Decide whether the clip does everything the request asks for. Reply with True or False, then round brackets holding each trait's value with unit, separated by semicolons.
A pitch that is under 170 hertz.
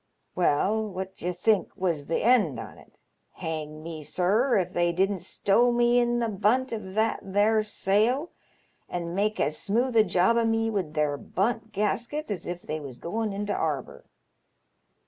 False (200 Hz)